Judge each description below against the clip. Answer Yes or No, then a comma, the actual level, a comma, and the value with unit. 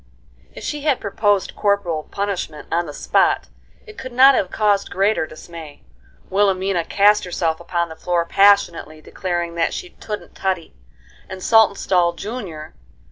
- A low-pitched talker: No, high, 190 Hz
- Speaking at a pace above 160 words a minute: No, average, 140 wpm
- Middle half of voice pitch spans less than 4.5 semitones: Yes, average, 3.3 semitones